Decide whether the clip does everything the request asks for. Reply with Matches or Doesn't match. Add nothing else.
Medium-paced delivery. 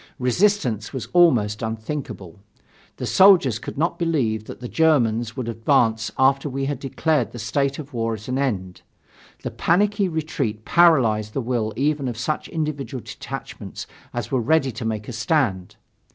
Matches